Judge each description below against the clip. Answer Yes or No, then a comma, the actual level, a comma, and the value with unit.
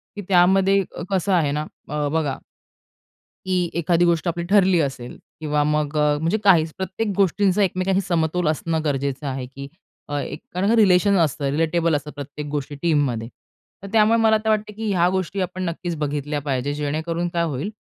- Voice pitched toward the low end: No, medium, 165 Hz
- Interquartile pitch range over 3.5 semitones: Yes, average, 4.2 semitones